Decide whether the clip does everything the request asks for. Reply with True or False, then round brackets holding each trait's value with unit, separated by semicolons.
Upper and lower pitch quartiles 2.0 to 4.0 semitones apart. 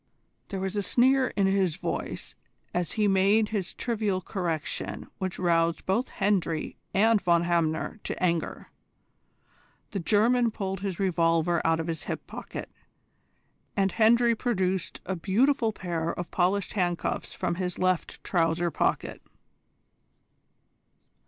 True (3.4 semitones)